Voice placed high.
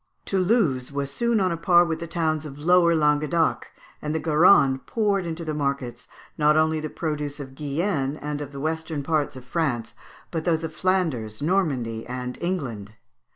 No: medium, 155 Hz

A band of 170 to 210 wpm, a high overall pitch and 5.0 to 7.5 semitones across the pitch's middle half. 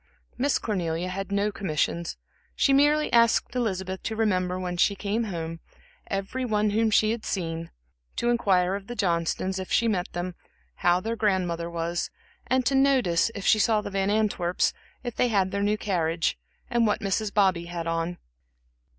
No: average, 175 wpm; high, 195 Hz; average, 3.8 semitones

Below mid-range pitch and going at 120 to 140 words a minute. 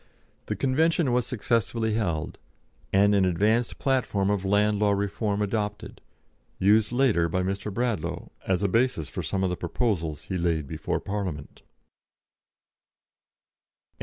Yes: low, 100 Hz; slow, 135 wpm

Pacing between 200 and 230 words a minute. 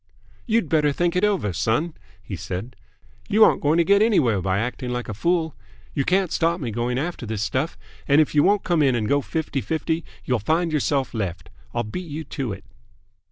Yes: fast, 205 wpm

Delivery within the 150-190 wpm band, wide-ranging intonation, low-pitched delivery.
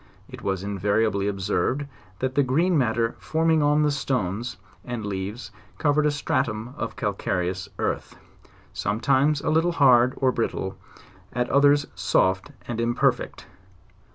No: slow, 135 wpm; wide, 5.8 semitones; low, 120 Hz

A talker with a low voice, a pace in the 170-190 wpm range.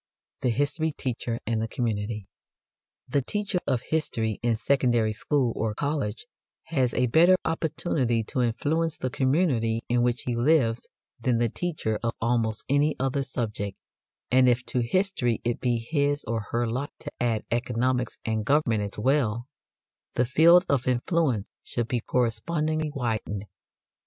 No: low, 125 Hz; average, 150 wpm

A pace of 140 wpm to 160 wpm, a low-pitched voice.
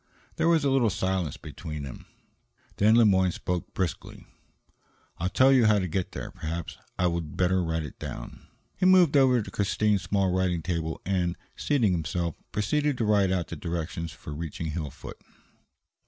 No: average, 170 wpm; very low, 95 Hz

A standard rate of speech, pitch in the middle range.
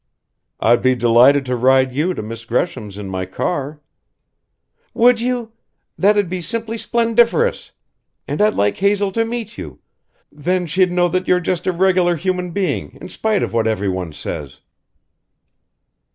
Yes: average, 155 wpm; medium, 175 Hz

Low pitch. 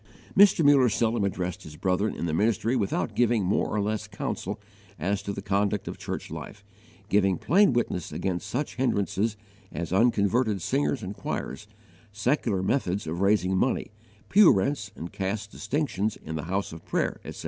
Yes: low, 105 Hz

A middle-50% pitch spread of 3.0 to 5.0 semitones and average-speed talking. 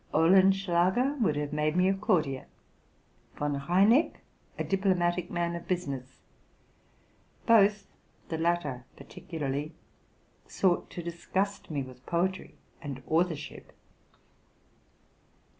No: average, 4.3 semitones; slow, 100 wpm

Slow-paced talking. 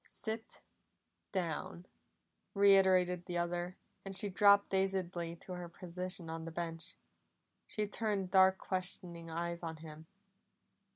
Yes: slow, 120 wpm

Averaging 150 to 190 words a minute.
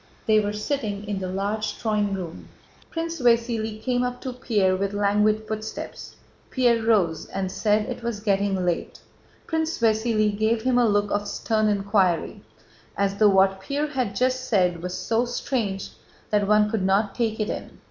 Yes: average, 170 wpm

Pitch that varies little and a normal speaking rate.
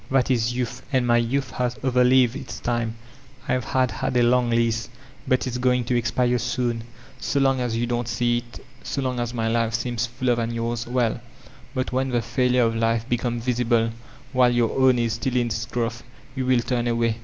No: narrow, 1.4 semitones; fast, 210 wpm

